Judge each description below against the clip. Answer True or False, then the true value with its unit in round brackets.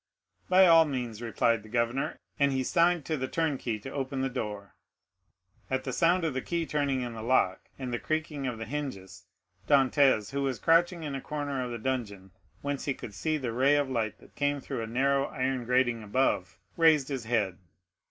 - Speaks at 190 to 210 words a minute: True (200 wpm)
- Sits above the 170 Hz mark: False (130 Hz)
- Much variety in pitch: False (3.6 semitones)